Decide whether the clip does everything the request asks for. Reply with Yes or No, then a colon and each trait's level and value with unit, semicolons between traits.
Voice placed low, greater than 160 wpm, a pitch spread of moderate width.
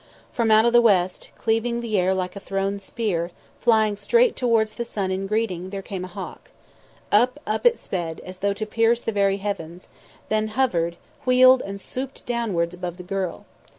No: high, 205 Hz; average, 185 wpm; average, 3.8 semitones